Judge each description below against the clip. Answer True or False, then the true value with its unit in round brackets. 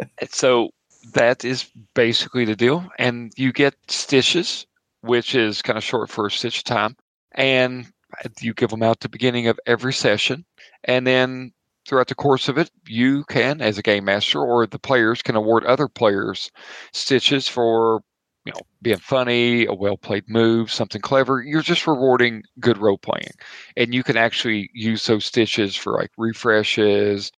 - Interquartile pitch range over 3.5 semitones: False (2.7 semitones)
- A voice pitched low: True (120 Hz)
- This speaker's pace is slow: False (170 wpm)